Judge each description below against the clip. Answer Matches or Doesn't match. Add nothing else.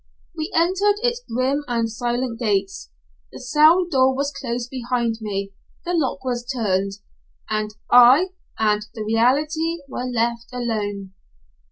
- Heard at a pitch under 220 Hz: Doesn't match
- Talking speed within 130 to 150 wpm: Matches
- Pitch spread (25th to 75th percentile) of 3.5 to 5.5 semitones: Matches